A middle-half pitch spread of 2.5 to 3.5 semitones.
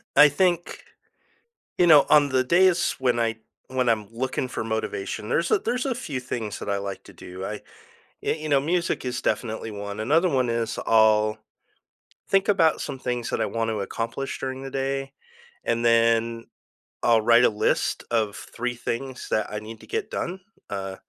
No: average, 4.4 semitones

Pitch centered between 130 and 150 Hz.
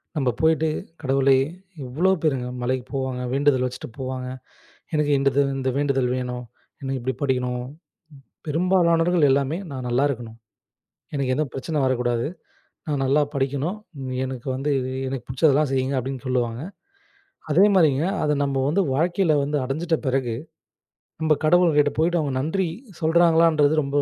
Yes: medium, 140 Hz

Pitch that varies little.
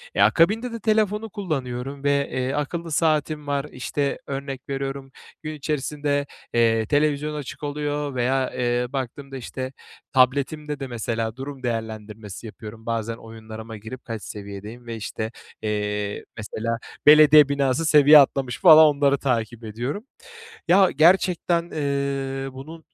No: average, 4.4 semitones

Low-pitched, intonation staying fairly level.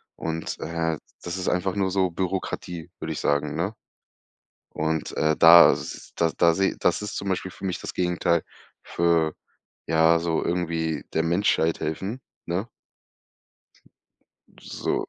Yes: very low, 85 Hz; narrow, 2.2 semitones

